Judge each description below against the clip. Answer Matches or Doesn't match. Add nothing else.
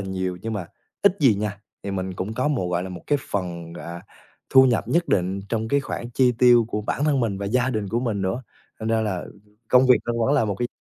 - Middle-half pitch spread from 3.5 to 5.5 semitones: Matches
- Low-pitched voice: Matches